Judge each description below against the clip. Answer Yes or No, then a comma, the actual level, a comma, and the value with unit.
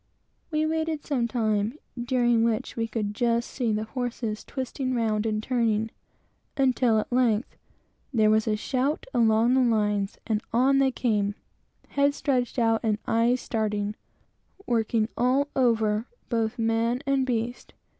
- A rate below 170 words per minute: Yes, average, 145 wpm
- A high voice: Yes, high, 230 Hz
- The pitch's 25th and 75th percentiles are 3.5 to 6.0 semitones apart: No, average, 2.7 semitones